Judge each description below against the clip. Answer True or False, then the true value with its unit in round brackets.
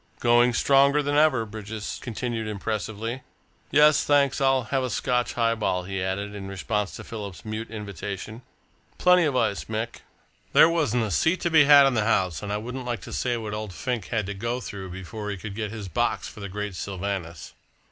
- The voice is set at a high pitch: False (110 Hz)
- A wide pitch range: False (3.8 semitones)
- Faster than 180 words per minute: True (200 wpm)